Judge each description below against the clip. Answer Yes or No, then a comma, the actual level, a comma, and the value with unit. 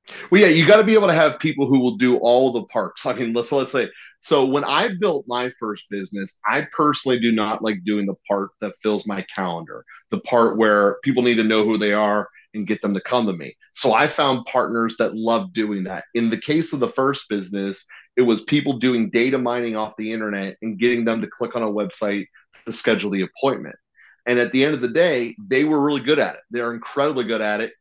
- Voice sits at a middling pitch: No, low, 115 Hz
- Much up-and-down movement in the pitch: No, average, 3.4 semitones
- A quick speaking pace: Yes, fast, 240 wpm